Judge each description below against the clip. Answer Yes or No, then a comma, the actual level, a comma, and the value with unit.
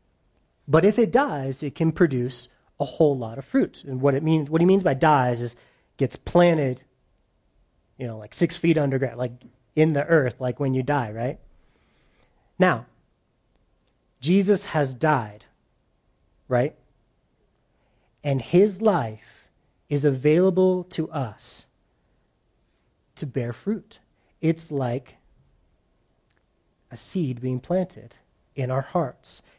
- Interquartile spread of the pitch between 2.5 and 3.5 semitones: No, average, 4.8 semitones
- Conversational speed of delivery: No, slow, 130 wpm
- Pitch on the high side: No, low, 135 Hz